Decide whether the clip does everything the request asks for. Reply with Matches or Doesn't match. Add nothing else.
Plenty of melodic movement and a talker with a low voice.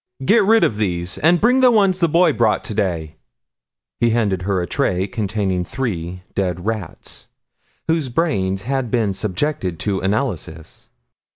Matches